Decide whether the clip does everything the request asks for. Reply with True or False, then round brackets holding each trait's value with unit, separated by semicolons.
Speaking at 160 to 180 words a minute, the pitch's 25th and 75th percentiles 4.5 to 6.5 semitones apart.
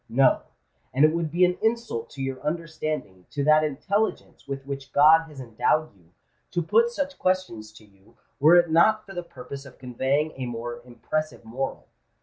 True (170 wpm; 5.2 semitones)